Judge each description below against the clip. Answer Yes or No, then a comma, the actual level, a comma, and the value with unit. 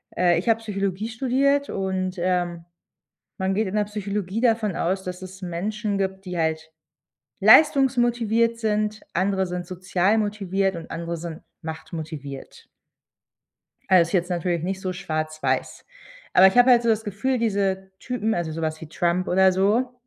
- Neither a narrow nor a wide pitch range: Yes, average, 3.6 semitones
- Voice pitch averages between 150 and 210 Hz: Yes, high, 190 Hz